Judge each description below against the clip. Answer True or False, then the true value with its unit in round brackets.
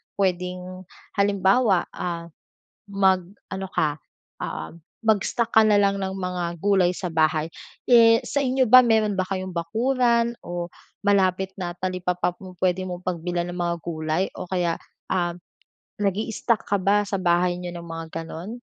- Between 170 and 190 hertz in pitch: True (185 Hz)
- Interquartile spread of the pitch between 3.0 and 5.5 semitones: False (2.6 semitones)